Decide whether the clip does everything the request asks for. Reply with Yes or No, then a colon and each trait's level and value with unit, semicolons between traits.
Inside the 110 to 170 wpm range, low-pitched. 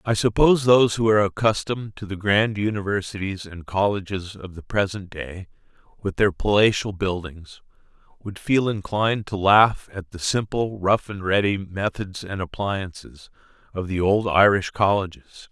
Yes: average, 150 wpm; low, 100 Hz